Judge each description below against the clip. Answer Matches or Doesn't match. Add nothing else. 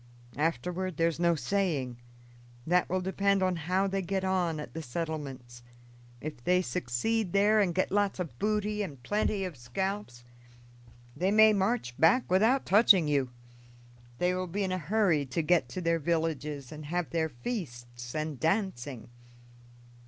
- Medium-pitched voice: Matches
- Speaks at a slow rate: Doesn't match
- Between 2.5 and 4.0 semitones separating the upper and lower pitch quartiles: Doesn't match